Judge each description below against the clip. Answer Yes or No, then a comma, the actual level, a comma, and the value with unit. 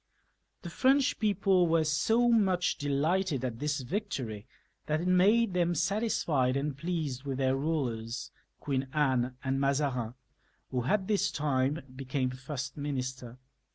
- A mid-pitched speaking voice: Yes, medium, 145 Hz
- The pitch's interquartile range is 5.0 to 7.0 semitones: Yes, wide, 5.6 semitones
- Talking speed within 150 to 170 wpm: No, slow, 135 wpm